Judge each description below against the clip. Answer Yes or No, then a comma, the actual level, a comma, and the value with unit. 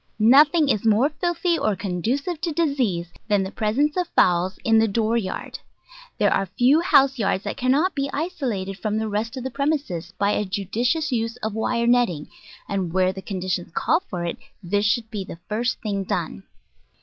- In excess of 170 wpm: Yes, average, 185 wpm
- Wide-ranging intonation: Yes, wide, 6.1 semitones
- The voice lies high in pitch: Yes, high, 225 Hz